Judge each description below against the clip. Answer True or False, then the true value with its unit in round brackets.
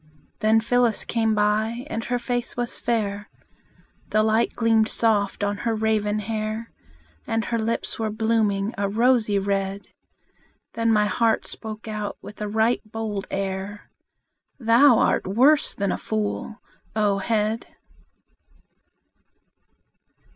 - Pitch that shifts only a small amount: True (1.8 semitones)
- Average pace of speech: False (125 wpm)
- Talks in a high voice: True (220 Hz)